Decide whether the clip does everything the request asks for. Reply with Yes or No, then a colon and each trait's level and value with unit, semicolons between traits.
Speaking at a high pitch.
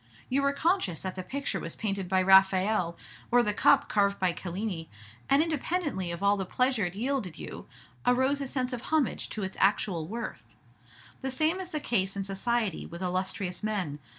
Yes: high, 205 Hz